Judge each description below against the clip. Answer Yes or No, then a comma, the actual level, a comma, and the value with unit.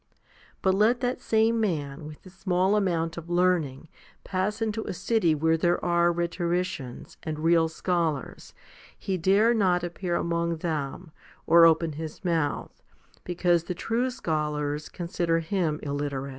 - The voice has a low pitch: No, medium, 170 Hz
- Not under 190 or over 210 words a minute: No, average, 145 wpm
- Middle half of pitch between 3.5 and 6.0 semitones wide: No, average, 2.9 semitones